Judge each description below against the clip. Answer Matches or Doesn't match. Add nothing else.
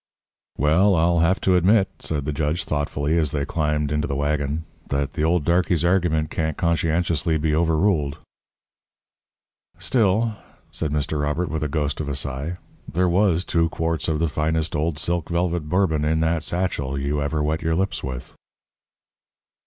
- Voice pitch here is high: Doesn't match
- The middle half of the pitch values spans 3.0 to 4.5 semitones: Doesn't match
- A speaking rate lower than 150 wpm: Doesn't match